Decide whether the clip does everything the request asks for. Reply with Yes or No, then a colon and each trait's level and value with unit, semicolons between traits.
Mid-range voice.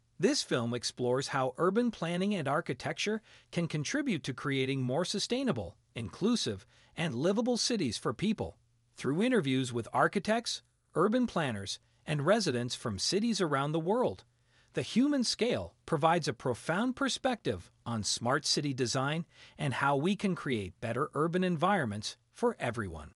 Yes: medium, 145 Hz